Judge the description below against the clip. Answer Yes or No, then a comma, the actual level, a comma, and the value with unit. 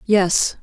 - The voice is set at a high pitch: Yes, high, 195 Hz